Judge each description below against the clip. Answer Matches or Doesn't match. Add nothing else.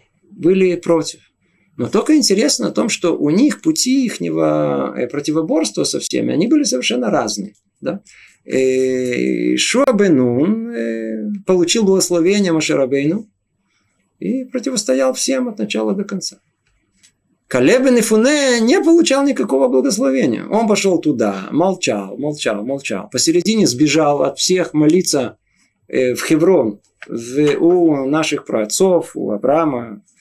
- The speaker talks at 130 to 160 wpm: Doesn't match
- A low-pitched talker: Doesn't match